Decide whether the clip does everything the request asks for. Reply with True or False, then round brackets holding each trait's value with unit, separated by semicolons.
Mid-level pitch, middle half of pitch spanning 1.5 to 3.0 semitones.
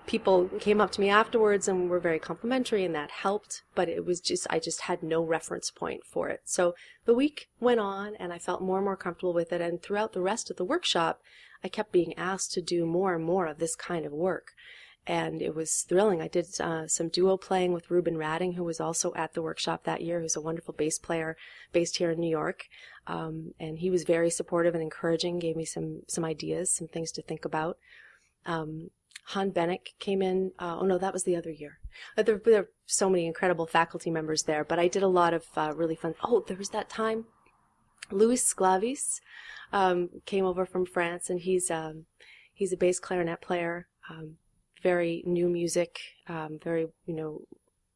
True (175 Hz; 2.5 semitones)